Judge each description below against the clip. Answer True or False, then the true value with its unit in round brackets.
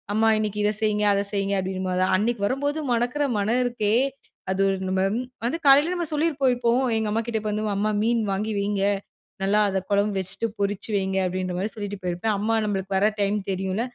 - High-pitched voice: True (210 Hz)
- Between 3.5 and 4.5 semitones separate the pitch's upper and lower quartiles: False (3.1 semitones)